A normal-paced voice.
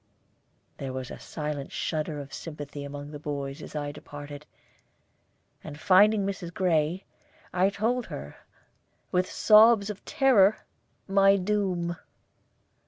No: slow, 120 wpm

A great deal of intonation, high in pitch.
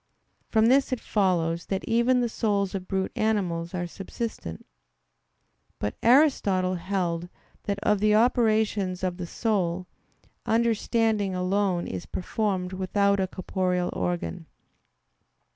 No: average, 3.3 semitones; high, 195 Hz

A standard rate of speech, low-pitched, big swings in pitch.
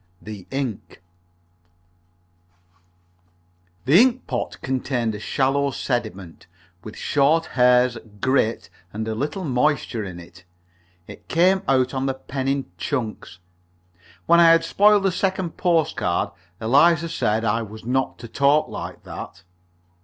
No: slow, 130 wpm; low, 130 Hz; wide, 6.1 semitones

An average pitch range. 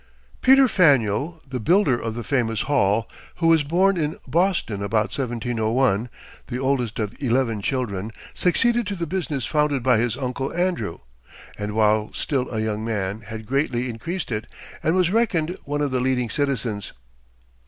No: wide, 6.1 semitones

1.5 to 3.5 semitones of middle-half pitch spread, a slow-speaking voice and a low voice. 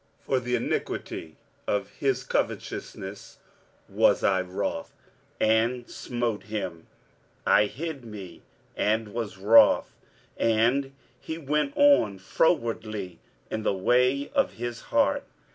No: average, 4.3 semitones; slow, 115 wpm; low, 115 Hz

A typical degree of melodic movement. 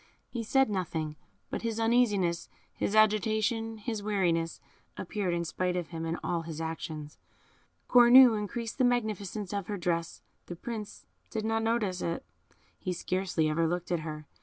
Yes: average, 4.9 semitones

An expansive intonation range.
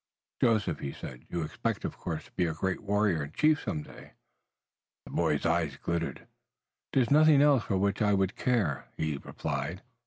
Yes: wide, 6.6 semitones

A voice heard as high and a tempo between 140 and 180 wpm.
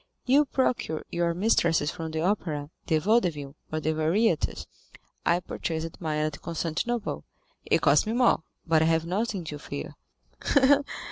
No: medium, 165 Hz; average, 145 wpm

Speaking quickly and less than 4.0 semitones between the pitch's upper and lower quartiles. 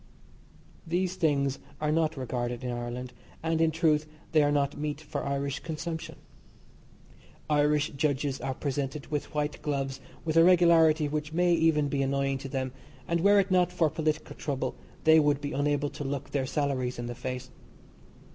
No: average, 170 wpm; average, 2.7 semitones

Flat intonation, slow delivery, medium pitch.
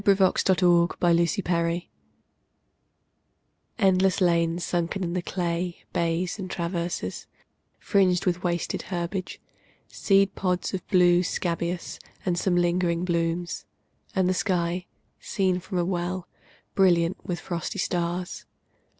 Yes: narrow, 1.4 semitones; slow, 120 wpm; medium, 175 Hz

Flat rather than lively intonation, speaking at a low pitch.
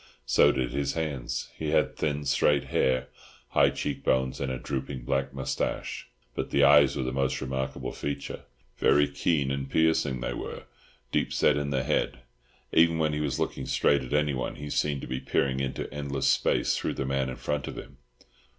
Yes: narrow, 1.8 semitones; very low, 70 Hz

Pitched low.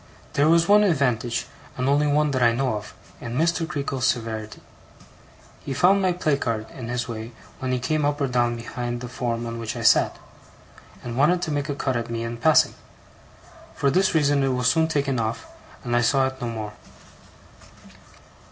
Yes: low, 130 Hz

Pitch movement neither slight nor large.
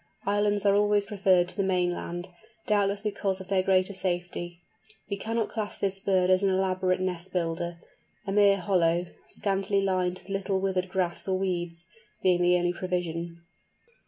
No: narrow, 1.9 semitones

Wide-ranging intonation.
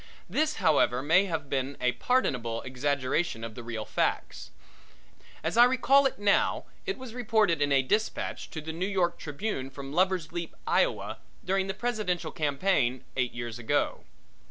Yes: wide, 7.4 semitones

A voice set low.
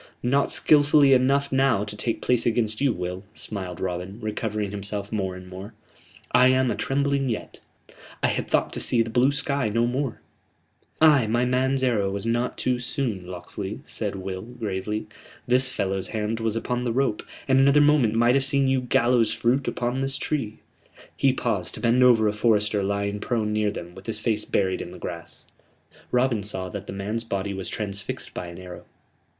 Yes: low, 115 Hz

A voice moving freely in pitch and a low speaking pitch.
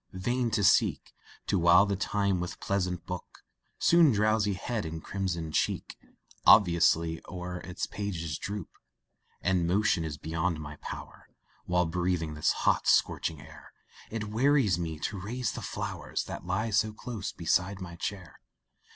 No: average, 3.5 semitones; very low, 90 Hz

